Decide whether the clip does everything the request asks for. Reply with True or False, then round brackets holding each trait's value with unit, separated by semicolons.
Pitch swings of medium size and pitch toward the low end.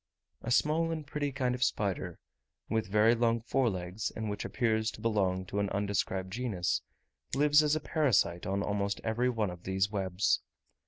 True (4.5 semitones; 110 Hz)